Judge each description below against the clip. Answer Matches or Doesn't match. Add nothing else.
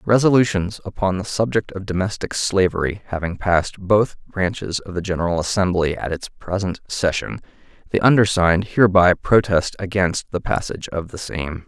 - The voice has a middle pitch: Doesn't match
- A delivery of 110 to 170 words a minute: Matches